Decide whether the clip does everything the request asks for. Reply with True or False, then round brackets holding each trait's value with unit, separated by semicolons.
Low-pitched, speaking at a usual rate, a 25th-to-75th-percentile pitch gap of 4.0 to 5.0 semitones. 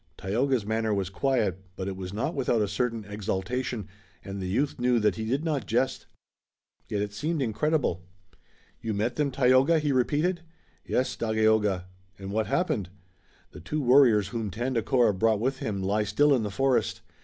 True (115 Hz; 170 wpm; 4.5 semitones)